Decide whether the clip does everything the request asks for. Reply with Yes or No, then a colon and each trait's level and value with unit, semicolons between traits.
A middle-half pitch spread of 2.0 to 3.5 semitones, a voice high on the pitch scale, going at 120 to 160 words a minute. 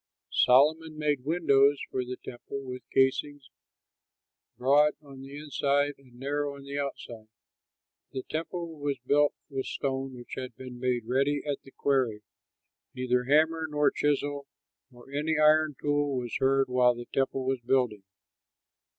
No: narrow, 2.4 semitones; medium, 140 Hz; average, 145 wpm